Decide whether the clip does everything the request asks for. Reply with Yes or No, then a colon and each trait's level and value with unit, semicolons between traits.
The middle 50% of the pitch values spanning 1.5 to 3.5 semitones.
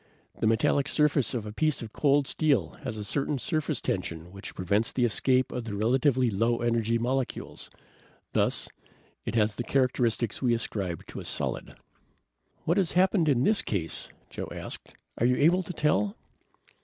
No: average, 4.9 semitones